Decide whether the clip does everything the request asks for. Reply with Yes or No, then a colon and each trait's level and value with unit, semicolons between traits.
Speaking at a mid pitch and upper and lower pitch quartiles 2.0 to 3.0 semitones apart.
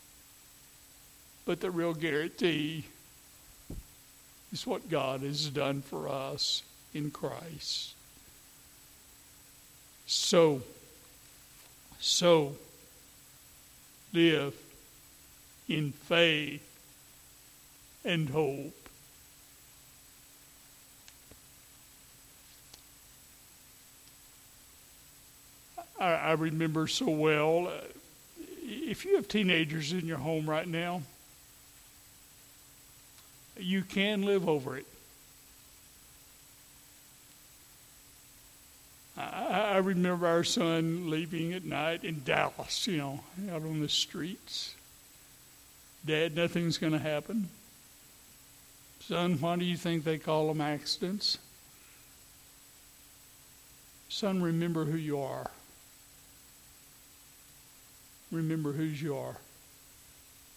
Yes: medium, 160 Hz; average, 2.7 semitones